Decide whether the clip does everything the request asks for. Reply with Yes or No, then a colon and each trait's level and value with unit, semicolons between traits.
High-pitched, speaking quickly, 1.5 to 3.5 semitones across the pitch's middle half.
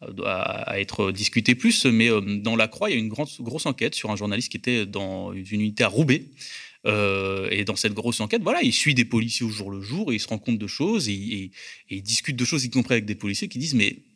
No: low, 110 Hz; fast, 265 wpm; average, 3.2 semitones